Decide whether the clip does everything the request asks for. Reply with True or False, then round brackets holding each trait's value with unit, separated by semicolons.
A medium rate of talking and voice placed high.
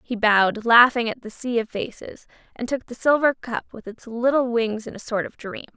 False (230 wpm; 235 Hz)